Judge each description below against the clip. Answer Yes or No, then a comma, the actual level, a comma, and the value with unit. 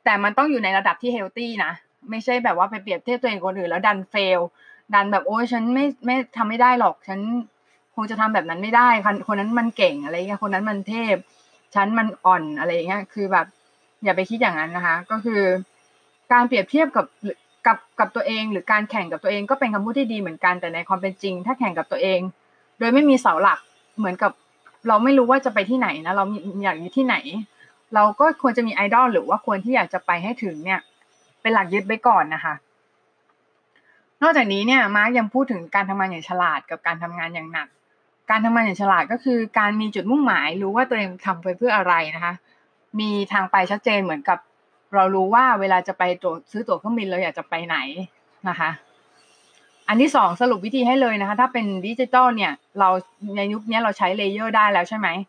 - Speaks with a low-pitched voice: No, high, 210 Hz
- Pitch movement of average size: Yes, average, 4.2 semitones